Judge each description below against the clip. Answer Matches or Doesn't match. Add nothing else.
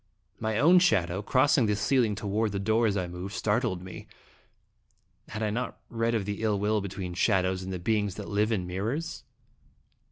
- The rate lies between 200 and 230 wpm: Doesn't match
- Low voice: Matches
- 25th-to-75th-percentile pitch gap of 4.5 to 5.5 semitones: Doesn't match